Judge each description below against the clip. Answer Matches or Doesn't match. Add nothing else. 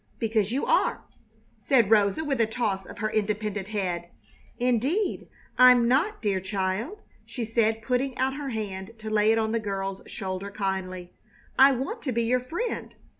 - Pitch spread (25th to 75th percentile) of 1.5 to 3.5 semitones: Doesn't match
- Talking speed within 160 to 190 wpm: Matches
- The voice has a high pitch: Matches